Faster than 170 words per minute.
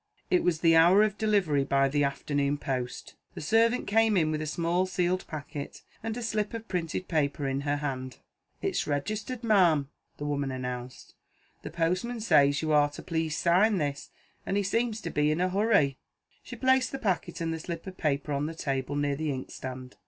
Yes: average, 195 wpm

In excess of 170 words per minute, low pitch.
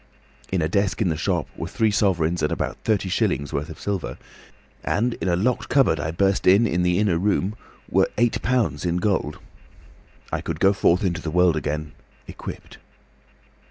Yes: average, 180 wpm; very low, 90 Hz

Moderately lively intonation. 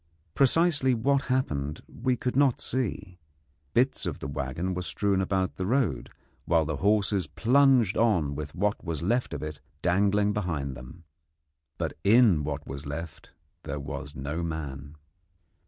No: wide, 7.8 semitones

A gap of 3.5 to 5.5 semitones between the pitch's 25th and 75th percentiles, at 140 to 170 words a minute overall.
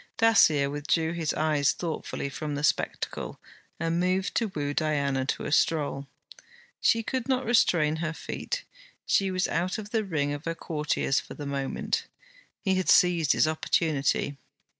Yes: average, 4.2 semitones; average, 160 wpm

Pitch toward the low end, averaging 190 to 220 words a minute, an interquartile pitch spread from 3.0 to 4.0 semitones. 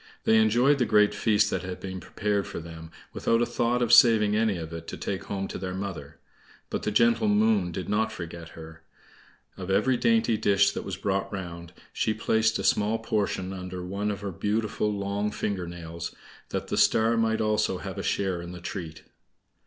Yes: low, 100 Hz; average, 200 wpm; average, 3.3 semitones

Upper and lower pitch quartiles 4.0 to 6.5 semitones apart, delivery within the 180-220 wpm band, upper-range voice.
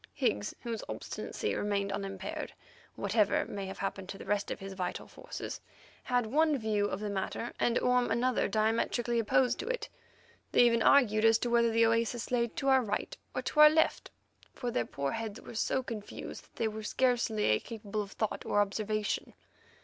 No: average, 2.9 semitones; average, 190 wpm; high, 220 Hz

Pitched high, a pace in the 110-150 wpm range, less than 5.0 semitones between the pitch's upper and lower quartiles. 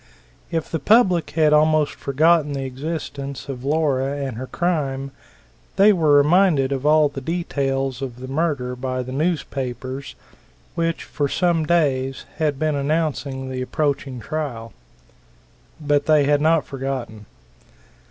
No: medium, 145 Hz; slow, 135 wpm; average, 2.9 semitones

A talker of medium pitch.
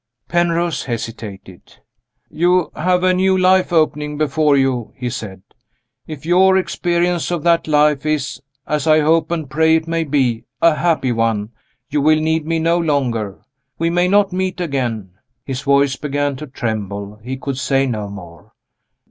Yes: medium, 150 Hz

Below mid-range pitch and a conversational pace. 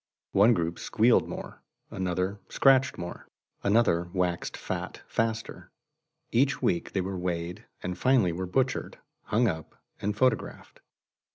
No: low, 100 Hz; slow, 125 wpm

